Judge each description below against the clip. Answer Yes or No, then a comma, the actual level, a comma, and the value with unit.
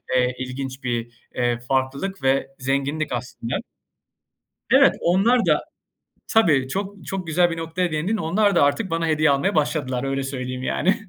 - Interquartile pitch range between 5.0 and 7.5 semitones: Yes, wide, 5.5 semitones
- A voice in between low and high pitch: Yes, medium, 145 Hz